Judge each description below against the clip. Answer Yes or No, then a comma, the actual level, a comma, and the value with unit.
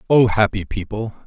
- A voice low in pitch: Yes, low, 105 Hz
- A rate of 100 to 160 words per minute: Yes, average, 140 wpm